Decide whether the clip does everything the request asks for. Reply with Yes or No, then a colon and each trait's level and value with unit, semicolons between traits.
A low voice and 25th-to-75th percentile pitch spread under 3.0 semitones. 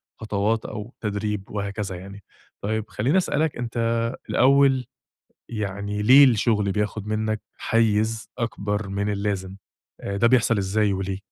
Yes: low, 105 Hz; narrow, 2.4 semitones